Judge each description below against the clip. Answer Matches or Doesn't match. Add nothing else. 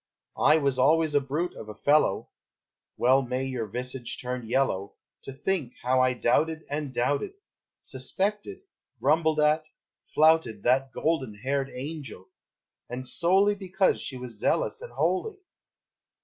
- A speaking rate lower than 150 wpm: Matches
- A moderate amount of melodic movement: Matches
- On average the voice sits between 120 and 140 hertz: Matches